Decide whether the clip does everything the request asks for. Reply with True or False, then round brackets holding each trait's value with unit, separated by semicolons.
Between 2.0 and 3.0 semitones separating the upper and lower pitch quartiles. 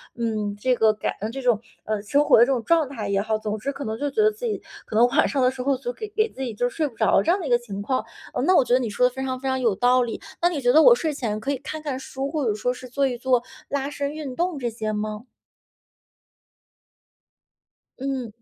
False (4.0 semitones)